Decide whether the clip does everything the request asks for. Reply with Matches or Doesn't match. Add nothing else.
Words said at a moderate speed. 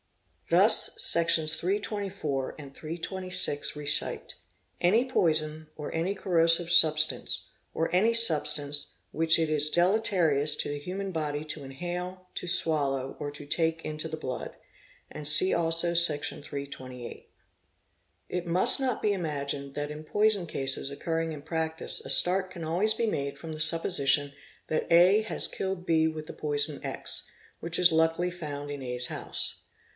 Matches